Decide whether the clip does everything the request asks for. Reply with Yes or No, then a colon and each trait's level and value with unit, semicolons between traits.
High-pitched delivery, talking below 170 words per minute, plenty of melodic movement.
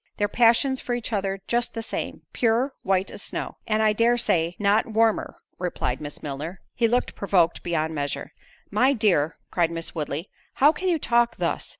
No: high, 210 Hz; average, 175 wpm; wide, 5.9 semitones